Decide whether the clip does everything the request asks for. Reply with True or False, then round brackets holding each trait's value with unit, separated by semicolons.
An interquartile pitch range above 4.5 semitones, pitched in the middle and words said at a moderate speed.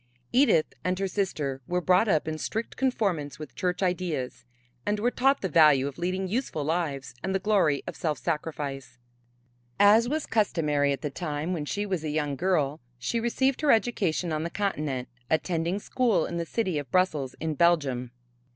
True (5.1 semitones; 170 Hz; 180 wpm)